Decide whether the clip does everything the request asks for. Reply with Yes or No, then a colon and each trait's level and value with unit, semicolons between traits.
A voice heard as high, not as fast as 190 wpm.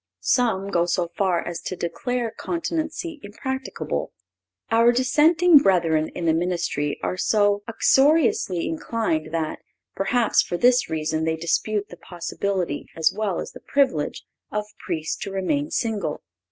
Yes: high, 195 Hz; average, 140 wpm